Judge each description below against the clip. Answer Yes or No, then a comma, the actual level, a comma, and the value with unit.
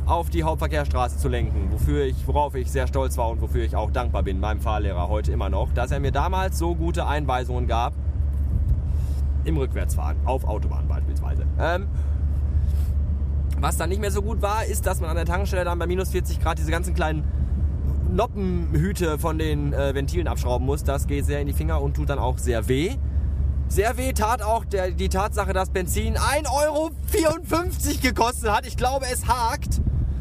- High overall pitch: No, very low, 75 Hz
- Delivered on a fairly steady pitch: Yes, narrow, 1.6 semitones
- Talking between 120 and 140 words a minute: No, average, 185 wpm